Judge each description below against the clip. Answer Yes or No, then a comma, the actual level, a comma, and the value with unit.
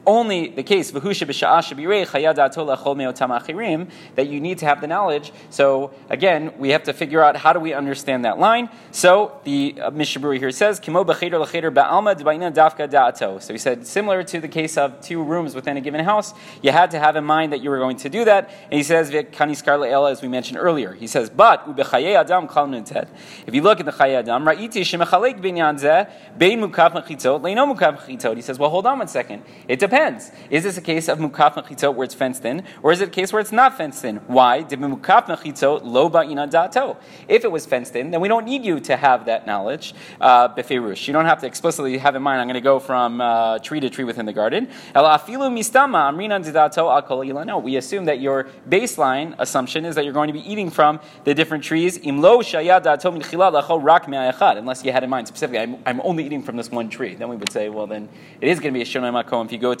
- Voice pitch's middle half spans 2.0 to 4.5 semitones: No, average, 5.0 semitones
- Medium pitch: Yes, medium, 155 Hz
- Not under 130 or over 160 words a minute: No, average, 190 wpm